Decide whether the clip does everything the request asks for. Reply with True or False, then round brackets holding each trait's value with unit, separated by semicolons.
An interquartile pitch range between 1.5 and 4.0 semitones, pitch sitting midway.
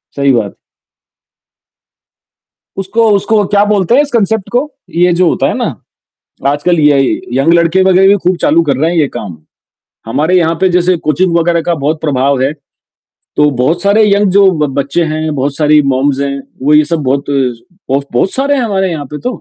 False (5.3 semitones; 165 Hz)